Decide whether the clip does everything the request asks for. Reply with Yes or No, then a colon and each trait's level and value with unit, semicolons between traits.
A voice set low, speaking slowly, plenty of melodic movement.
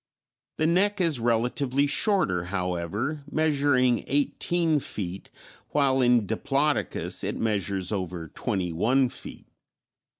Yes: low, 125 Hz; slow, 105 wpm; wide, 7.0 semitones